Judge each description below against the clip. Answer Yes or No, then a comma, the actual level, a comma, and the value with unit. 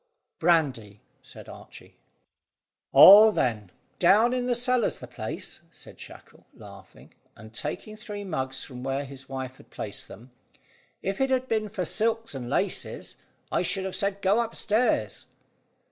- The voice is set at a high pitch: No, medium, 180 Hz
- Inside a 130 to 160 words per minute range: Yes, average, 145 wpm